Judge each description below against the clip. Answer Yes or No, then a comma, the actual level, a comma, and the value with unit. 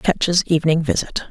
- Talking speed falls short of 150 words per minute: Yes, average, 140 wpm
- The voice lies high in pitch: No, medium, 160 Hz